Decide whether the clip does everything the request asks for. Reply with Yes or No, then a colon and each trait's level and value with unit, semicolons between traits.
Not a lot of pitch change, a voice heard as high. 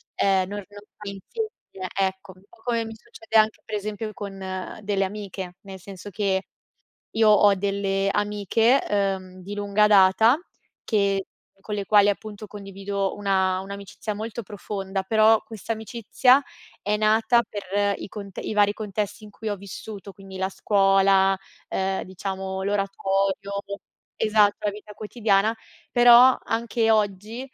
Yes: narrow, 1.7 semitones; high, 205 Hz